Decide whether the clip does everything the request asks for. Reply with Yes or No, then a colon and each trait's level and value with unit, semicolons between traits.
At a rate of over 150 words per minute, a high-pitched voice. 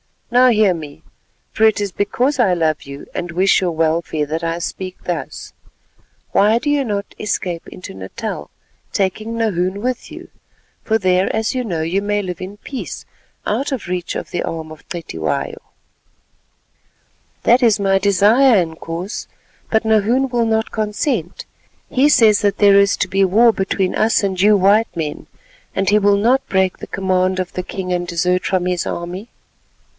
Yes: average, 170 wpm; high, 195 Hz